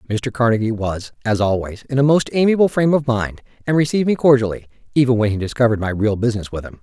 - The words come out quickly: Yes, fast, 220 wpm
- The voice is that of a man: Yes, male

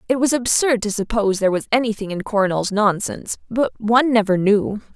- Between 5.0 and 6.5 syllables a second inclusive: Yes, 6.0 syllables/s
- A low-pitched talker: No, high, 215 Hz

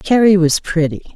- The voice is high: No, medium, 180 Hz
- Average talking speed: Yes, average, 155 wpm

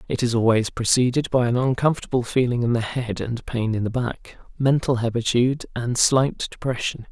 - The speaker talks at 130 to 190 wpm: Yes, average, 175 wpm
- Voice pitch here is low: Yes, low, 120 Hz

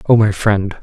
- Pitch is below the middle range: Yes, low, 105 Hz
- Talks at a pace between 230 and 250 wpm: No, fast, 220 wpm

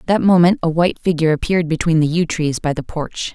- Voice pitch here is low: No, medium, 165 Hz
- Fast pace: Yes, fast, 235 wpm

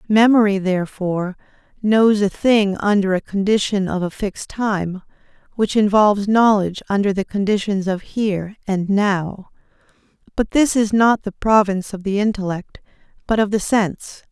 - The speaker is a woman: Yes, female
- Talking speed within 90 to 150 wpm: Yes, average, 145 wpm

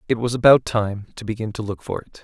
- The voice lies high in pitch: No, low, 110 Hz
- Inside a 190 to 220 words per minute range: No, fast, 270 wpm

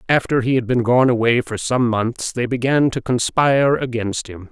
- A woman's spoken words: No, male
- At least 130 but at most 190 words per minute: No, average, 200 wpm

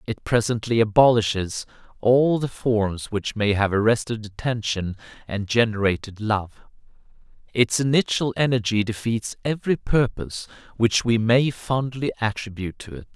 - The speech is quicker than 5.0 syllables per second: No, 4.8 syllables/s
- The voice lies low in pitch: Yes, low, 115 Hz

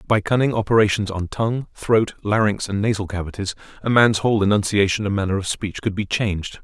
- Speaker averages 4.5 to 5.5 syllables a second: No, 5.9 syllables/s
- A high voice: No, low, 105 Hz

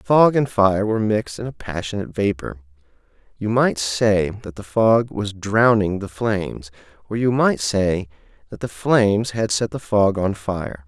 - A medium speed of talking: Yes, average, 180 wpm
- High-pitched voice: No, low, 105 Hz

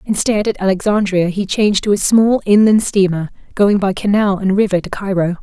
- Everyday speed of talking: Yes, average, 190 wpm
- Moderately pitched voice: No, high, 200 Hz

